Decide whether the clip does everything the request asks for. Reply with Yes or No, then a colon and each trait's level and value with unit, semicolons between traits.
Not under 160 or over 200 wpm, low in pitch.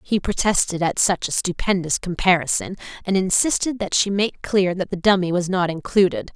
No: average, 180 wpm; high, 190 Hz